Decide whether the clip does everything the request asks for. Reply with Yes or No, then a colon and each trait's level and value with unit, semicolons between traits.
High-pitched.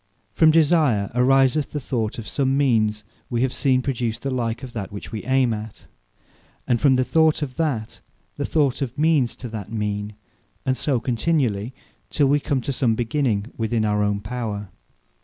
No: low, 125 Hz